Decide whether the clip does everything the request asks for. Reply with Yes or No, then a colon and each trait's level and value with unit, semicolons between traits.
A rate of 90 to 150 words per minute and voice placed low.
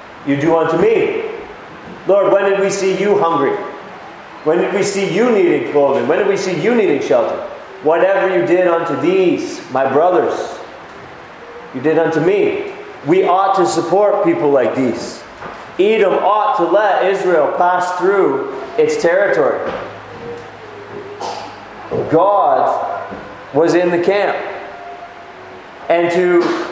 No: slow, 135 wpm; high, 195 Hz